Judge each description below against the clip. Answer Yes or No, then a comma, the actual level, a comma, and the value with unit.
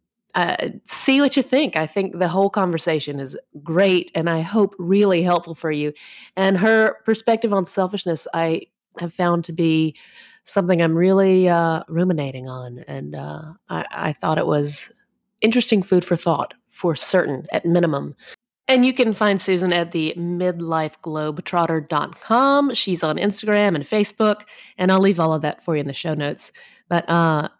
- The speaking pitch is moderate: Yes, medium, 175 Hz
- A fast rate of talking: No, average, 165 wpm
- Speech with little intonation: No, average, 4.2 semitones